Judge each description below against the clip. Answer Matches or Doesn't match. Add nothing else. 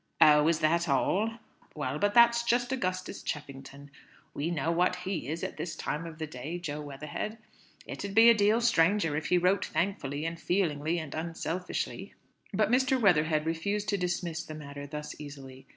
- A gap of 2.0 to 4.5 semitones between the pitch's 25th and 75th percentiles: Doesn't match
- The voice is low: Doesn't match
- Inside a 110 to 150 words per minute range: Doesn't match